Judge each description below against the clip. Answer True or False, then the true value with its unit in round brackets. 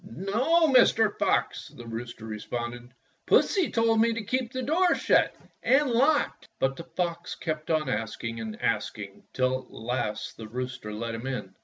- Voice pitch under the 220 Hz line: True (135 Hz)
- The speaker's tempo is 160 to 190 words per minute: True (165 wpm)